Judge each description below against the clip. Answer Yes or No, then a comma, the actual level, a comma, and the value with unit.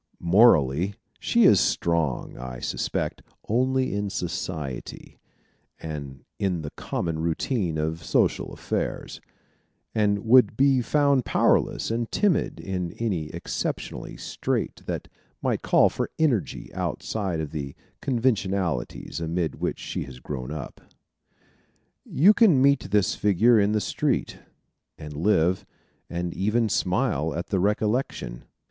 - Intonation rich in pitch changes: Yes, wide, 6.3 semitones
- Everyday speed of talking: No, slow, 125 wpm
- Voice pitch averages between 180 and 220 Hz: No, very low, 95 Hz